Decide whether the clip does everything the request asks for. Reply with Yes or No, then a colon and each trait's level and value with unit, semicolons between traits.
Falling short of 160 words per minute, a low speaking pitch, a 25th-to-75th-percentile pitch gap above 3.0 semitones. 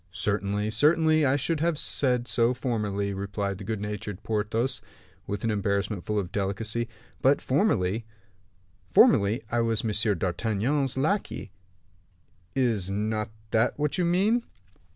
Yes: slow, 135 wpm; low, 110 Hz; average, 4.6 semitones